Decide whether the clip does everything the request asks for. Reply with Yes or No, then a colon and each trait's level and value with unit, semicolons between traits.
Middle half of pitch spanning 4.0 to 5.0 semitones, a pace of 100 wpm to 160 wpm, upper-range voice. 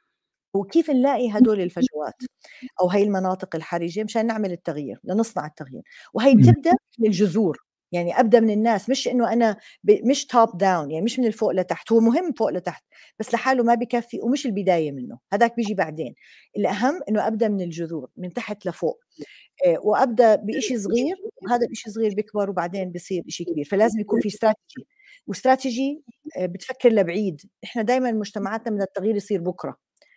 Yes: average, 4.6 semitones; average, 155 wpm; high, 215 Hz